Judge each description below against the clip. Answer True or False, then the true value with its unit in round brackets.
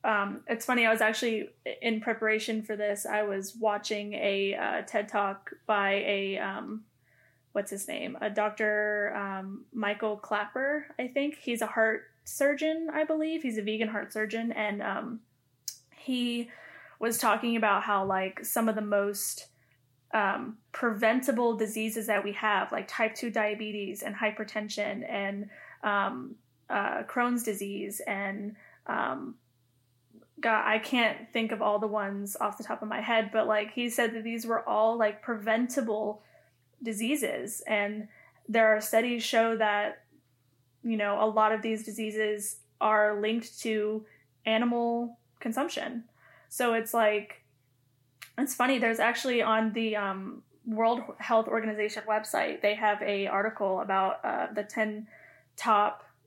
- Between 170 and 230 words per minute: False (145 wpm)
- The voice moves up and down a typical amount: False (1.9 semitones)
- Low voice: False (215 Hz)